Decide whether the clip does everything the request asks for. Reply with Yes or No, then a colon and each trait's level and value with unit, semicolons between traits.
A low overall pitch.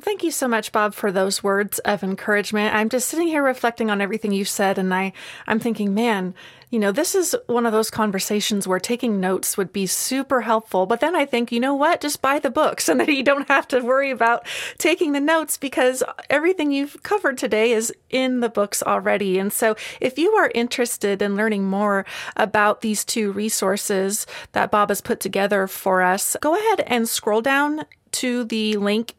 No: high, 225 Hz